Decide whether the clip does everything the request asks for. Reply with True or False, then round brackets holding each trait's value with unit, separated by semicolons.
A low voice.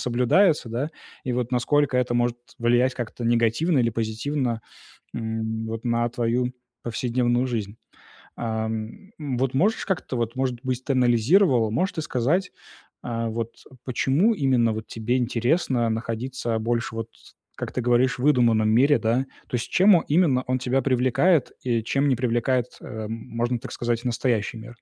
True (120 Hz)